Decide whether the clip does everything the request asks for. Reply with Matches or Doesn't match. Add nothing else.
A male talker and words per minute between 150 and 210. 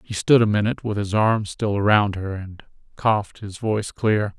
Matches